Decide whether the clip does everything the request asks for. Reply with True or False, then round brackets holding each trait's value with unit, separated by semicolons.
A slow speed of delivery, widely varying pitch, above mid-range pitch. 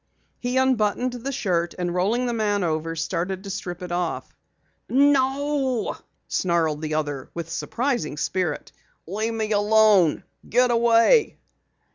True (130 wpm; 6.1 semitones; 205 Hz)